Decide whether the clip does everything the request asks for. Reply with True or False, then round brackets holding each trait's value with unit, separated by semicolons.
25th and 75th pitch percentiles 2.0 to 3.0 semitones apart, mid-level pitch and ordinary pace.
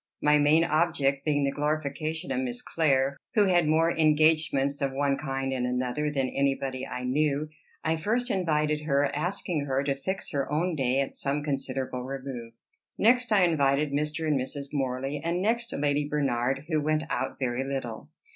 True (2.7 semitones; 145 Hz; 175 wpm)